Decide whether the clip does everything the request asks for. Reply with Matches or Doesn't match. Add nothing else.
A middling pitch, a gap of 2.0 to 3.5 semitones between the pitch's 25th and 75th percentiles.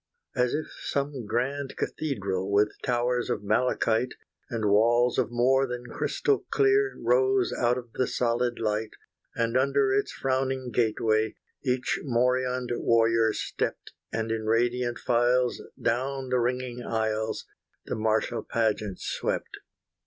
Doesn't match